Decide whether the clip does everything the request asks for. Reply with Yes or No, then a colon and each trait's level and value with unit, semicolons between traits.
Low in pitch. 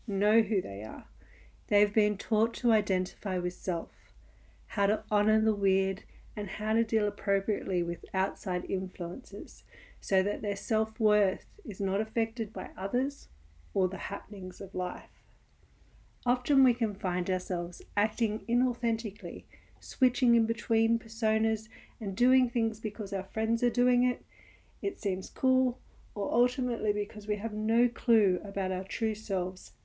No: high, 210 Hz